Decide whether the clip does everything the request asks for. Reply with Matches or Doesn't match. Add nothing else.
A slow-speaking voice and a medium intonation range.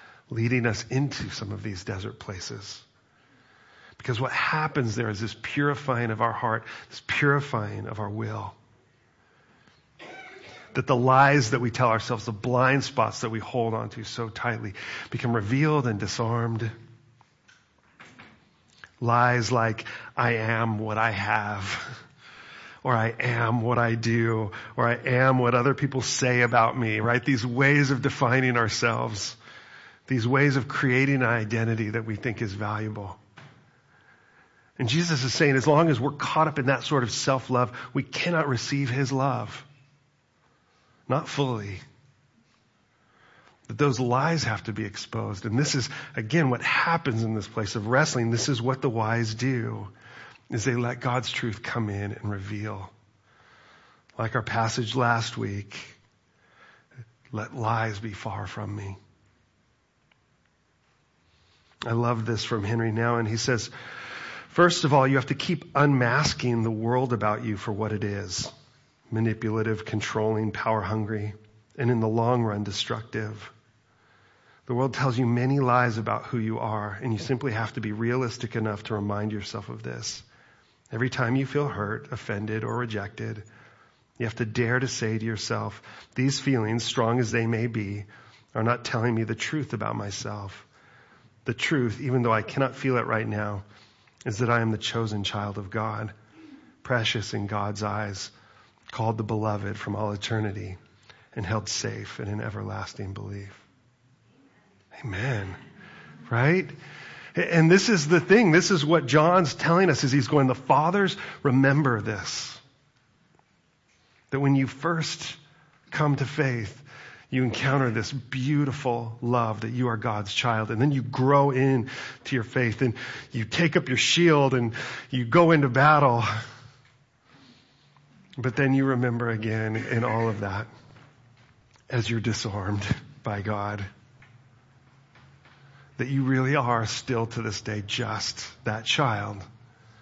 Doesn't match